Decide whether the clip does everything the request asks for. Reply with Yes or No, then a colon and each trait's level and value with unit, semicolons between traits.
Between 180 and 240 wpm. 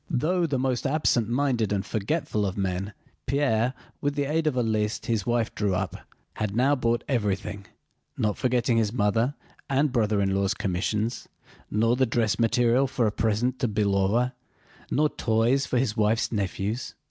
No: average, 165 wpm